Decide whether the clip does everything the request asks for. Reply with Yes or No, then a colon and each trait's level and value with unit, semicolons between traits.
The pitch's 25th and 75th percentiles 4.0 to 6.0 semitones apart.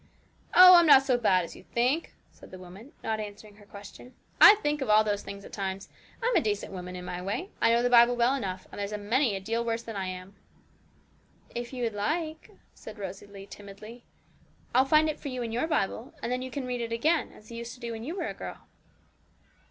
Yes: average, 4.3 semitones